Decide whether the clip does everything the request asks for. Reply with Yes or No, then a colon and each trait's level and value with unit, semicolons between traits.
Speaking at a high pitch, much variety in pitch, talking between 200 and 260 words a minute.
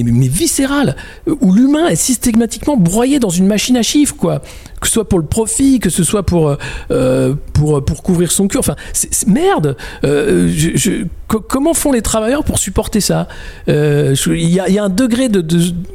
Yes: high, 195 Hz; wide, 7.7 semitones; average, 205 wpm